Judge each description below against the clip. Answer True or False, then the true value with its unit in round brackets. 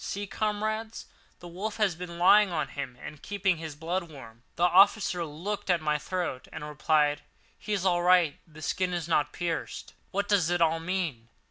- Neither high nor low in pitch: True (175 Hz)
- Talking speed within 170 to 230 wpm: True (190 wpm)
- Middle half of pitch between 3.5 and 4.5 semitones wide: True (3.9 semitones)